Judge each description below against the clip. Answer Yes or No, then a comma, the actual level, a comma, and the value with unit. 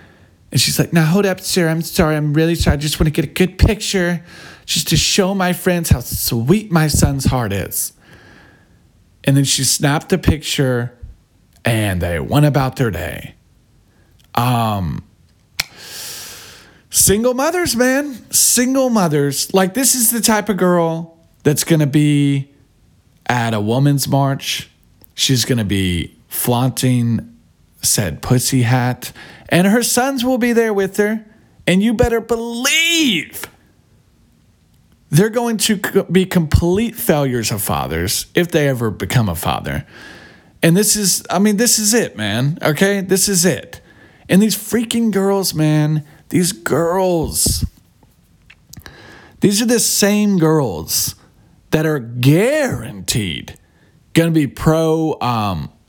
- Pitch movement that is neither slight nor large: No, wide, 8.4 semitones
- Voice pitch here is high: No, medium, 155 Hz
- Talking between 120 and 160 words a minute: Yes, average, 140 wpm